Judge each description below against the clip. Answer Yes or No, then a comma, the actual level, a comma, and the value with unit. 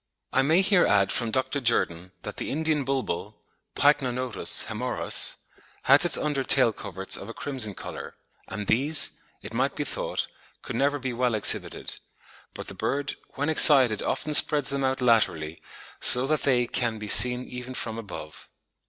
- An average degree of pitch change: Yes, average, 4.1 semitones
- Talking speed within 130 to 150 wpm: No, average, 165 wpm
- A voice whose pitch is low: Yes, low, 130 Hz